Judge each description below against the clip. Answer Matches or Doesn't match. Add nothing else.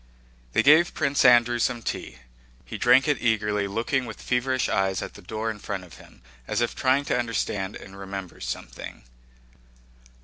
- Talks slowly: Doesn't match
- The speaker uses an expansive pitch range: Doesn't match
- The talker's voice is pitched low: Matches